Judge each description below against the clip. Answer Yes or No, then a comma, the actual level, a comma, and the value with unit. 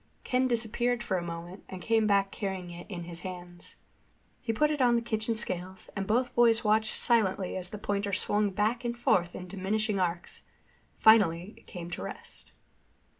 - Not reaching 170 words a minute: No, average, 180 wpm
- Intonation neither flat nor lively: Yes, average, 3.8 semitones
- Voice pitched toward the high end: Yes, high, 205 Hz